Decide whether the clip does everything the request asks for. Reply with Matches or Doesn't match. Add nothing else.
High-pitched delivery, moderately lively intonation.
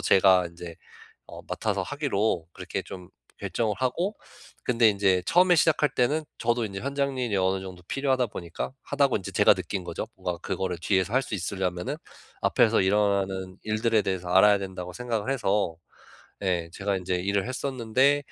Doesn't match